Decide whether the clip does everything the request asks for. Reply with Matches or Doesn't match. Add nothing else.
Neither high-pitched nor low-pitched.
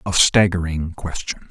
Doesn't match